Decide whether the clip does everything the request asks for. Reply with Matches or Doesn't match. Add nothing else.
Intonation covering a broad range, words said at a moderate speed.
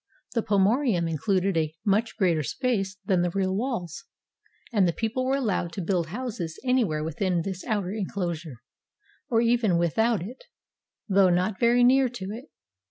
Doesn't match